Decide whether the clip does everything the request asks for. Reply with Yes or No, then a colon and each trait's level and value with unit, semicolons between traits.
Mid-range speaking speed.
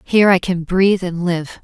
No: fast, 220 wpm